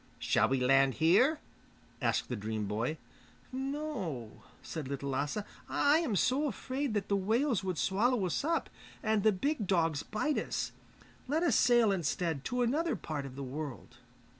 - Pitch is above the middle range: Yes, high, 195 Hz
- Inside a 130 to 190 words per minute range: Yes, average, 165 wpm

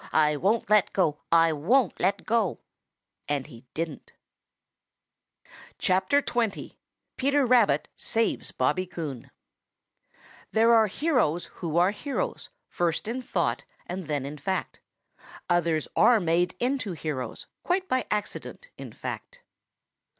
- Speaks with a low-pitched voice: No, medium, 185 Hz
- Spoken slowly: Yes, slow, 120 wpm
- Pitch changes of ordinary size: No, wide, 6.8 semitones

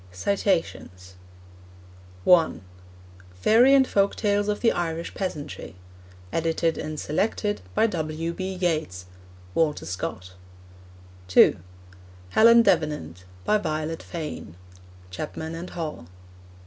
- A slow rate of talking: Yes, slow, 95 wpm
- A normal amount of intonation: Yes, average, 4.7 semitones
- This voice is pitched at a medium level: Yes, medium, 165 Hz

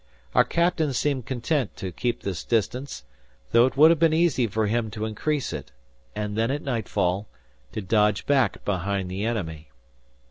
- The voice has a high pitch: No, low, 115 Hz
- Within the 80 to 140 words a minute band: No, average, 170 wpm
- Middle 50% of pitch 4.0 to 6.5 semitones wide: Yes, wide, 5.4 semitones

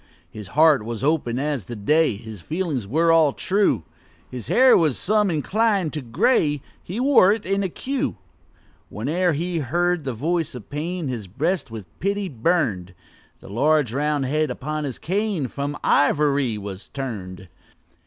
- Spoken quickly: No, average, 160 wpm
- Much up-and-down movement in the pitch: Yes, wide, 6.5 semitones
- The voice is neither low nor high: Yes, medium, 150 Hz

